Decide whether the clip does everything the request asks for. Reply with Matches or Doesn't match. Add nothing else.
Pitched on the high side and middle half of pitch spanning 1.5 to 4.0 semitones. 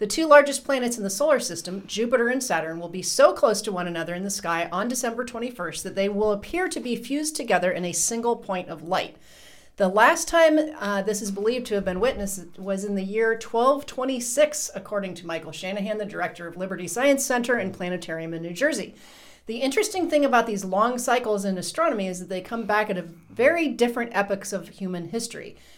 Doesn't match